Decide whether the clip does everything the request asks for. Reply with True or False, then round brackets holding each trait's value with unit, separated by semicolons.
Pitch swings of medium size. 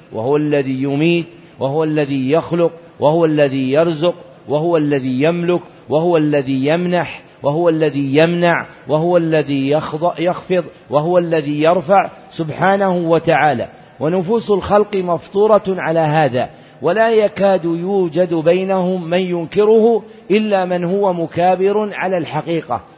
True (3.1 semitones)